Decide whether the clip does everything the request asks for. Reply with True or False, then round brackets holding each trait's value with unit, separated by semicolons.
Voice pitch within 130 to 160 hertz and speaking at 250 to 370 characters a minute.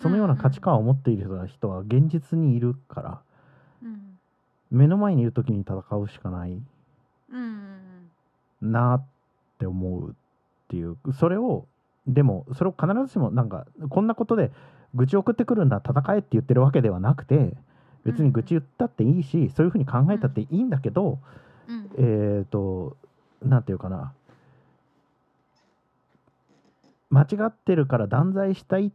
True (135 Hz; 295 characters per minute)